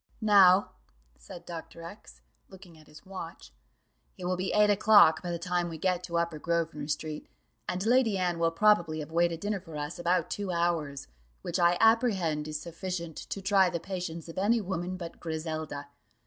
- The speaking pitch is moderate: Yes, medium, 175 Hz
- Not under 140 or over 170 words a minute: No, average, 180 wpm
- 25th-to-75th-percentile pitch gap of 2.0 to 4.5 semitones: Yes, average, 2.8 semitones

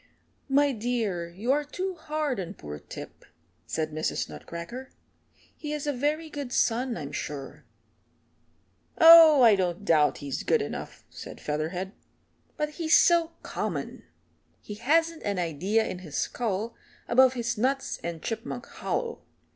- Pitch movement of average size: No, wide, 8.8 semitones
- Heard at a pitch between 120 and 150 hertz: No, high, 235 Hz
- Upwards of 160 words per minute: No, average, 140 wpm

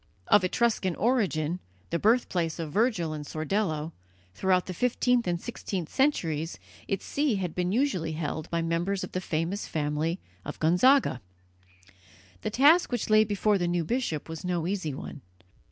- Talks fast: No, average, 160 wpm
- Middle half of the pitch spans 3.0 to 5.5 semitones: Yes, average, 4.9 semitones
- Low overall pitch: No, medium, 180 Hz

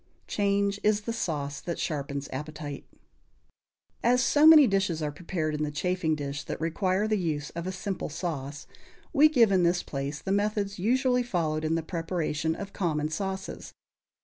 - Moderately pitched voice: Yes, medium, 175 Hz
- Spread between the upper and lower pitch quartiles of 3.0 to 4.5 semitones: No, average, 4.9 semitones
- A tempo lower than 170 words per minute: No, average, 175 wpm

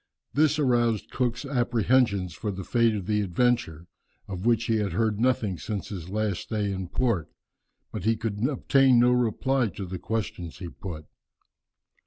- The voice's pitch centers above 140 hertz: No, low, 110 Hz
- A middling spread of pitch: Yes, average, 4.1 semitones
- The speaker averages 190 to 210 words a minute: No, average, 170 wpm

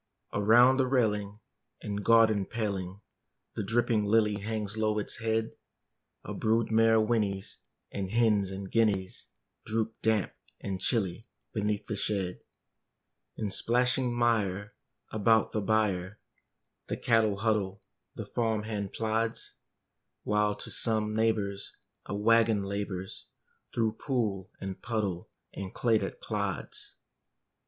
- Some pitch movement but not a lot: No, narrow, 2.0 semitones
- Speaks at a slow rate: Yes, slow, 120 wpm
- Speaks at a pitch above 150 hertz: No, low, 105 Hz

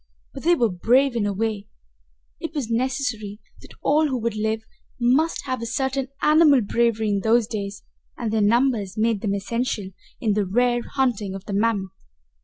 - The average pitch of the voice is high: Yes, high, 230 Hz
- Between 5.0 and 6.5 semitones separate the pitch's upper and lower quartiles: No, average, 3.8 semitones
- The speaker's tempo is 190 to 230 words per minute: No, average, 180 wpm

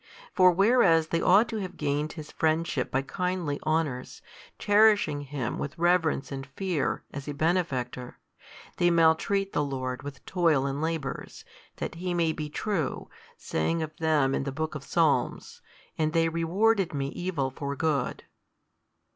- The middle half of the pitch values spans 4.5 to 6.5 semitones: No, average, 3.8 semitones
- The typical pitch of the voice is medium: Yes, medium, 160 Hz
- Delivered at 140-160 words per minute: Yes, average, 155 wpm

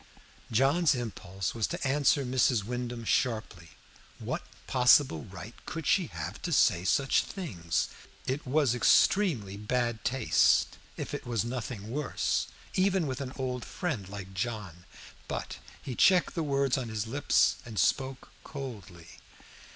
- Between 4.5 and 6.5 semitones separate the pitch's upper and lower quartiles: Yes, average, 4.9 semitones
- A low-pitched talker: Yes, low, 125 Hz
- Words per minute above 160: No, average, 140 wpm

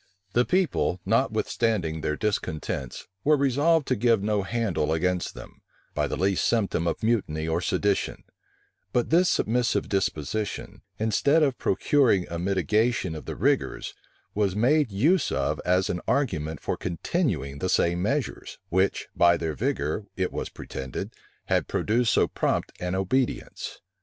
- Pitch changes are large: Yes, wide, 6.1 semitones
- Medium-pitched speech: No, low, 100 Hz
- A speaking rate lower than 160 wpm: Yes, average, 145 wpm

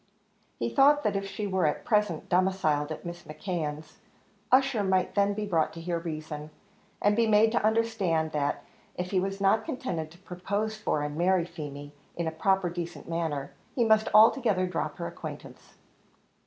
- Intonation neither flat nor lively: Yes, average, 4.6 semitones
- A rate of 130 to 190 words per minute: Yes, average, 175 wpm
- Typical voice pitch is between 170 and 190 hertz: Yes, medium, 185 Hz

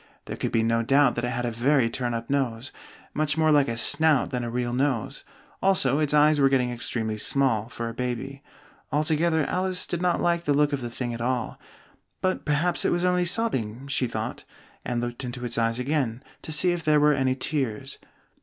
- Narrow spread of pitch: No, average, 4.0 semitones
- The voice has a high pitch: No, low, 135 Hz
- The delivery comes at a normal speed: No, fast, 210 wpm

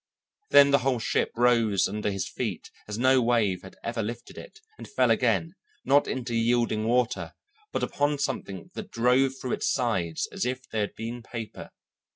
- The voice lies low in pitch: Yes, low, 120 Hz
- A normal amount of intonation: Yes, average, 3.1 semitones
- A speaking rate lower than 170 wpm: No, average, 180 wpm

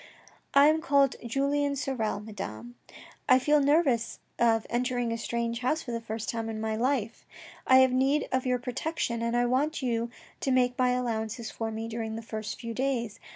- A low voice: No, high, 240 Hz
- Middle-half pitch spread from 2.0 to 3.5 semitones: Yes, average, 2.9 semitones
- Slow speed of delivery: No, average, 195 wpm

